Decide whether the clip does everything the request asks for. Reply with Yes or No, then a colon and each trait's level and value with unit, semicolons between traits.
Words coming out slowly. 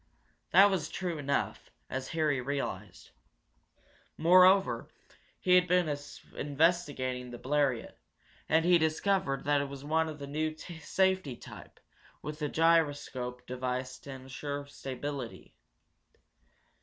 Yes: slow, 120 wpm